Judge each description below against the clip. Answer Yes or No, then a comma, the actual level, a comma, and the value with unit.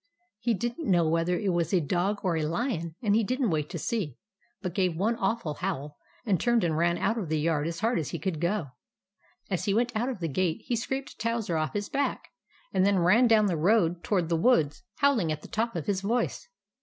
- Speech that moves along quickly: Yes, fast, 235 wpm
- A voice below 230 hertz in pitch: Yes, high, 190 Hz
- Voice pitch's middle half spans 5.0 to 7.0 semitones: Yes, wide, 5.5 semitones